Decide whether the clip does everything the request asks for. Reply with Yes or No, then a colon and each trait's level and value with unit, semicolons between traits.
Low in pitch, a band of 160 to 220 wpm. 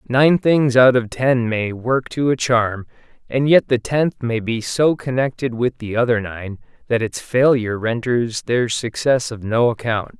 Yes: low, 120 Hz; average, 180 wpm